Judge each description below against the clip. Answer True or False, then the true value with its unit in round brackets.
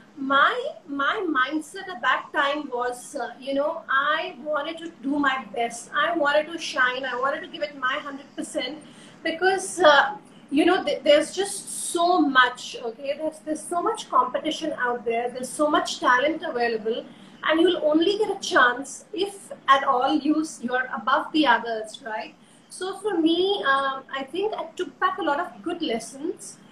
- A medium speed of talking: True (175 wpm)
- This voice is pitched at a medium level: False (290 Hz)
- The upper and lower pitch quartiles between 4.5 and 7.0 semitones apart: False (4.1 semitones)